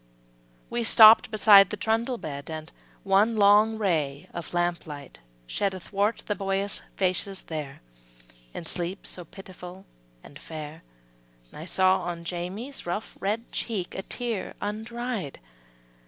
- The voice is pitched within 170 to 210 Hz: Yes, high, 190 Hz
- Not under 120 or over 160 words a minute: Yes, slow, 135 wpm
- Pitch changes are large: No, average, 4.0 semitones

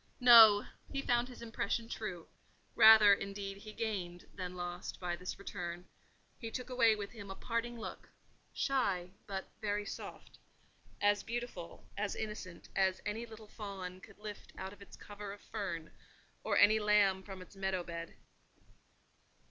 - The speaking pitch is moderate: No, high, 205 Hz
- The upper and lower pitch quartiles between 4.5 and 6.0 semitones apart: No, average, 2.9 semitones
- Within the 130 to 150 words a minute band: Yes, average, 145 wpm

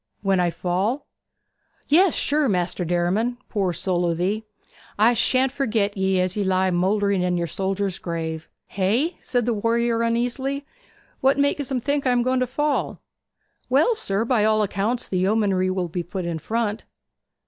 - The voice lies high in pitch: Yes, high, 210 Hz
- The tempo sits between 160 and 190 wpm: Yes, average, 170 wpm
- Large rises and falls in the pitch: No, average, 5.0 semitones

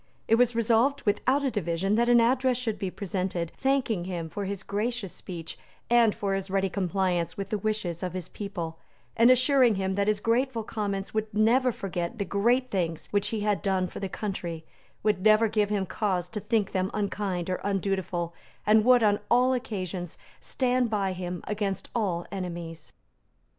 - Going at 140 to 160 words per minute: No, average, 180 wpm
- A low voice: No, high, 200 Hz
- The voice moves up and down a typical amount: Yes, average, 3.6 semitones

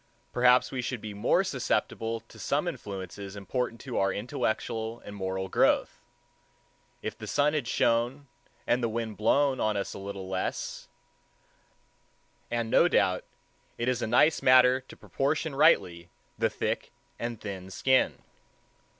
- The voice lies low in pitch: Yes, low, 115 Hz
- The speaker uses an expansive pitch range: No, average, 4.2 semitones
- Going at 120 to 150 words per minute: Yes, average, 145 wpm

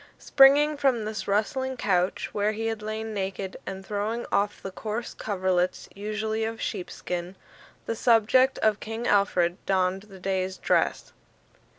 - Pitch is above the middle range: Yes, high, 210 Hz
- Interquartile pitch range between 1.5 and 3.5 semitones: Yes, average, 2.8 semitones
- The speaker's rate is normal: Yes, average, 145 wpm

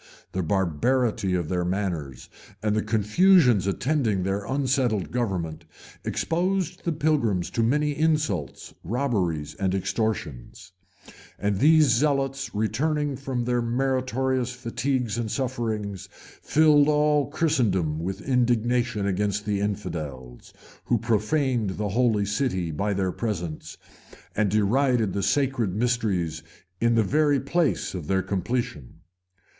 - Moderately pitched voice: No, low, 115 Hz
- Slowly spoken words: Yes, slow, 120 wpm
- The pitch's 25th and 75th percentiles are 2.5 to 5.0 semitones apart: No, wide, 5.6 semitones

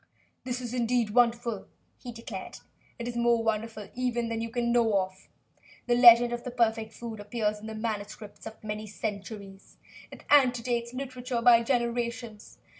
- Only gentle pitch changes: Yes, narrow, 1.9 semitones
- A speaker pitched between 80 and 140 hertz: No, high, 235 Hz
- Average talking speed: Yes, average, 160 wpm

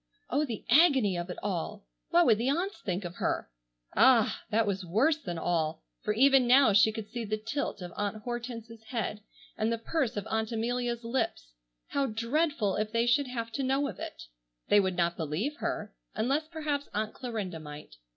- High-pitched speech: Yes, high, 225 Hz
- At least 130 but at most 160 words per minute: No, average, 190 wpm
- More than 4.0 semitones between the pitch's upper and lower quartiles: Yes, average, 4.5 semitones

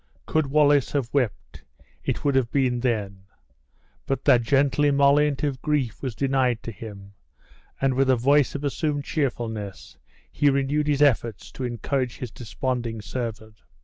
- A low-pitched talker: Yes, low, 130 Hz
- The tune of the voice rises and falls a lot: No, average, 3.5 semitones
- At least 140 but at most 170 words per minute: Yes, average, 150 wpm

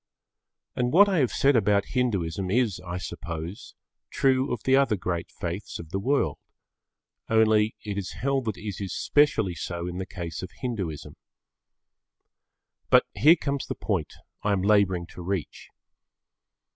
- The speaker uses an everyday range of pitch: No, wide, 5.9 semitones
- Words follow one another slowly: No, average, 155 wpm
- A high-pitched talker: No, low, 100 Hz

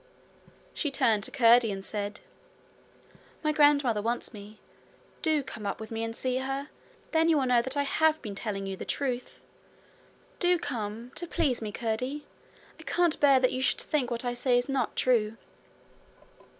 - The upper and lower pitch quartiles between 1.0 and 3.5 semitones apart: No, average, 4.4 semitones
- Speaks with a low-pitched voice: No, very high, 250 Hz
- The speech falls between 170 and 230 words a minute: Yes, average, 175 wpm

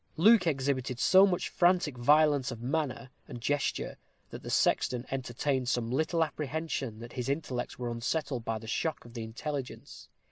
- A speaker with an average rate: Yes, average, 165 wpm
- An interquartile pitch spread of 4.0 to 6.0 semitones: Yes, average, 4.3 semitones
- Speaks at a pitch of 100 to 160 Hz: Yes, low, 135 Hz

